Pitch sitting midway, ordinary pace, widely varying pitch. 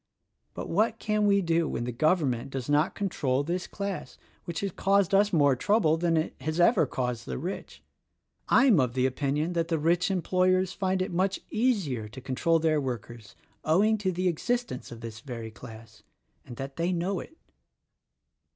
Yes: medium, 165 Hz; average, 180 wpm; wide, 6.6 semitones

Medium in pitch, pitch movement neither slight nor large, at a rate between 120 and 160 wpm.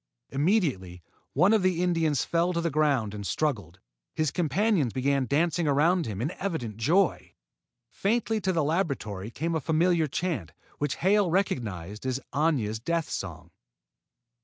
No: medium, 155 Hz; wide, 7.0 semitones; average, 145 wpm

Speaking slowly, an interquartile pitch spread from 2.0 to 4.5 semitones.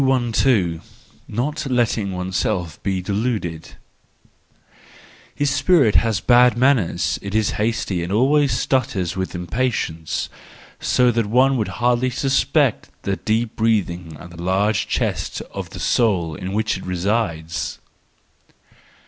No: slow, 125 wpm; average, 5.2 semitones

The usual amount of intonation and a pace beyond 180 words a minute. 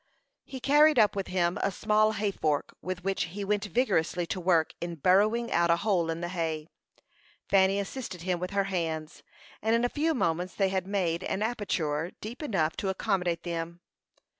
Yes: average, 3.6 semitones; average, 190 wpm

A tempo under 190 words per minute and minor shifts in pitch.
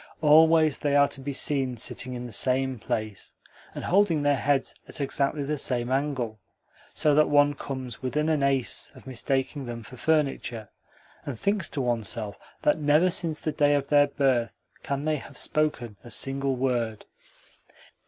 No: average, 170 wpm; average, 3.1 semitones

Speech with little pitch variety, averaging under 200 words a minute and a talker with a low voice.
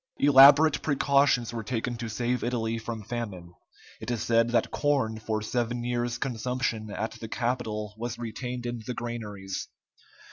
Yes: narrow, 1.9 semitones; average, 150 wpm; low, 120 Hz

